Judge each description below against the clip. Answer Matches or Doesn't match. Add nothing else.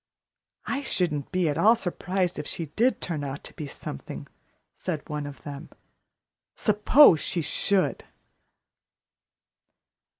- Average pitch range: Matches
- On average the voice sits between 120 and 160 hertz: Doesn't match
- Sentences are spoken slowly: Matches